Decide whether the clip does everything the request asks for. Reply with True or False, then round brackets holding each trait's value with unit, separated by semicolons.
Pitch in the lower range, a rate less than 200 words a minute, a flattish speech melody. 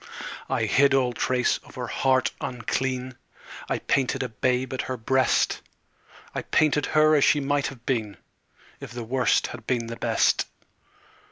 True (130 Hz; 160 wpm; 1.9 semitones)